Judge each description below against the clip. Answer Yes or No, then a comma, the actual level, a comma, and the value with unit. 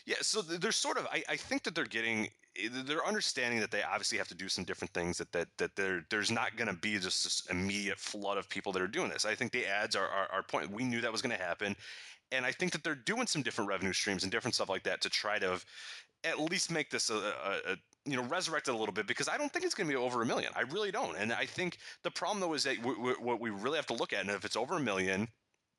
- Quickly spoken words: Yes, fast, 285 wpm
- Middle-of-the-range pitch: No, low, 125 Hz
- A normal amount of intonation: No, wide, 8.2 semitones